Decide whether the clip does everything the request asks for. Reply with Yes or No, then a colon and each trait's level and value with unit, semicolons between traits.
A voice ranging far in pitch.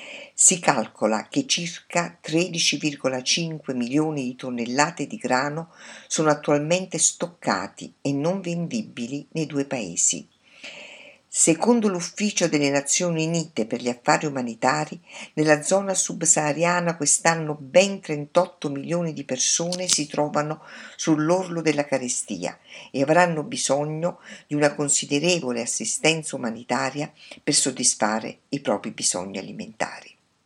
No: average, 3.7 semitones